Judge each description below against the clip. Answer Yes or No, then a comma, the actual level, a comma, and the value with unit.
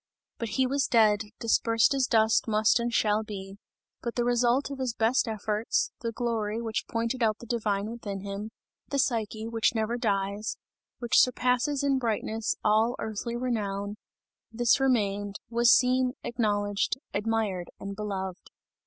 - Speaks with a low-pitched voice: No, high, 225 Hz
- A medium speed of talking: Yes, average, 150 wpm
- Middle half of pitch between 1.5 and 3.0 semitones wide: Yes, narrow, 2.5 semitones